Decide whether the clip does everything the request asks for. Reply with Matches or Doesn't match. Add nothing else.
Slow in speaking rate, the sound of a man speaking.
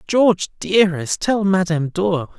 Matches